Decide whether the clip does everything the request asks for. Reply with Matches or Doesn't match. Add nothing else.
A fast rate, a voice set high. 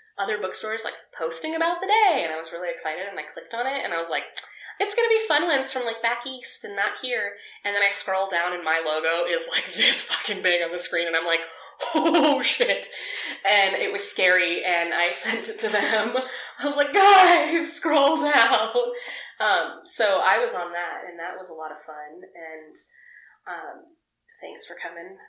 Matches